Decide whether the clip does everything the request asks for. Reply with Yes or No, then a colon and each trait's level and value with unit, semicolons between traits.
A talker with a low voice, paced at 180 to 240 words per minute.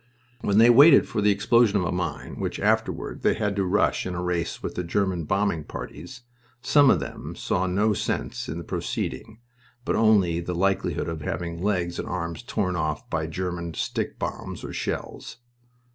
Yes: very low, 90 Hz; average, 185 wpm